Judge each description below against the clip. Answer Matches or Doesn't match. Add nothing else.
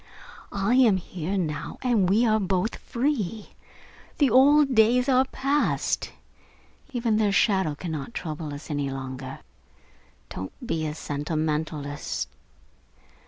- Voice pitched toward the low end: Doesn't match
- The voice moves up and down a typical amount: Doesn't match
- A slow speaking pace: Matches